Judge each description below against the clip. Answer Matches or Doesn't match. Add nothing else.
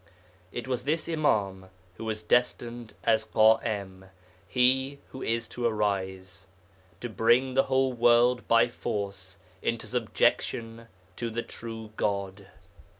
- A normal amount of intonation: Matches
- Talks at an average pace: Doesn't match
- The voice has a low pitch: Matches